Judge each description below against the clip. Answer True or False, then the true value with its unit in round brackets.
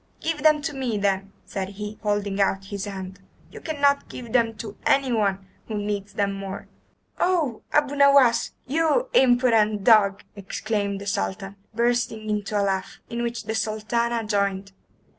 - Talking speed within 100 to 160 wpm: True (155 wpm)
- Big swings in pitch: False (3.5 semitones)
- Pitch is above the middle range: True (215 Hz)